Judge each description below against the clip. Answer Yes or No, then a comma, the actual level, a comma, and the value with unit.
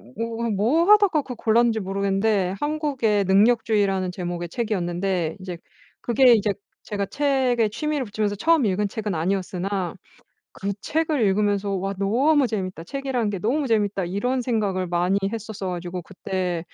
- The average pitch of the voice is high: Yes, high, 205 Hz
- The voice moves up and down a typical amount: Yes, average, 4.1 semitones